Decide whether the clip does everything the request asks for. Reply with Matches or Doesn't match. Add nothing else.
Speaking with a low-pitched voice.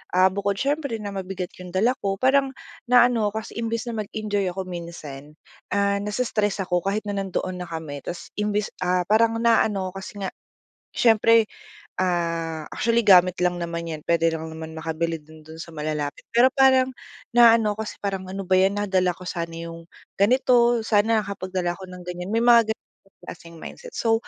Doesn't match